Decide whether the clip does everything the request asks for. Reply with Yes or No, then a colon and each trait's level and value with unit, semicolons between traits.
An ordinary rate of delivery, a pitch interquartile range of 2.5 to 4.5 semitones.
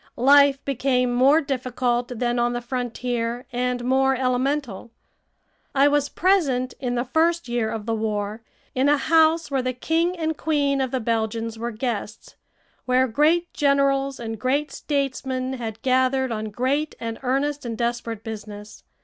Yes: average, 155 wpm; average, 2.9 semitones